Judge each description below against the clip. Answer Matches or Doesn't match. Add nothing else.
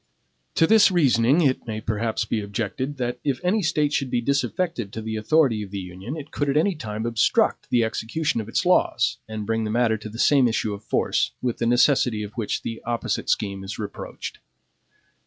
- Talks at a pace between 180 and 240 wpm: Matches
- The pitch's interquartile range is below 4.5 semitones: Doesn't match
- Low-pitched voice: Matches